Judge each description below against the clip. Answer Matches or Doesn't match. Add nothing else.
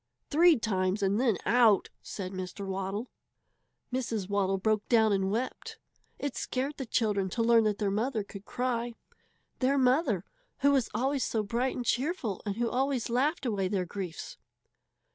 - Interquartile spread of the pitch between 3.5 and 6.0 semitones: Matches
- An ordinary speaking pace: Matches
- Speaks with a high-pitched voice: Matches